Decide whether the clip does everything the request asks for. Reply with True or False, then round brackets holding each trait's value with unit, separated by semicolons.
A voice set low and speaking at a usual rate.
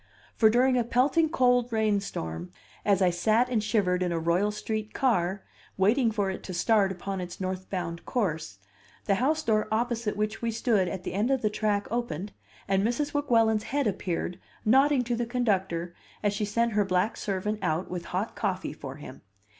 False (210 Hz; 185 wpm)